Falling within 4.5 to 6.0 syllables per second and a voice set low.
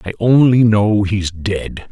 No: 3.5 syllables/s; low, 105 Hz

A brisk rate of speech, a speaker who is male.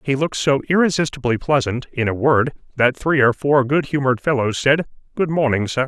No: average, 195 wpm; male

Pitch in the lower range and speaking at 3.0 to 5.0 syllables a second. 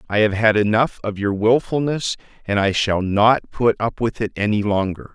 Yes: low, 110 Hz; 4.9 syllables/s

